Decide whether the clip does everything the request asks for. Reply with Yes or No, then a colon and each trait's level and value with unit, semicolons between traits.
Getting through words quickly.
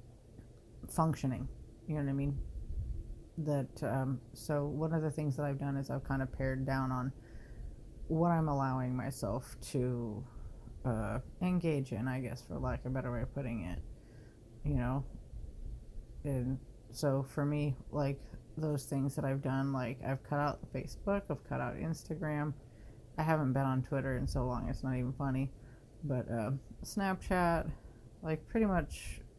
No: average, 165 wpm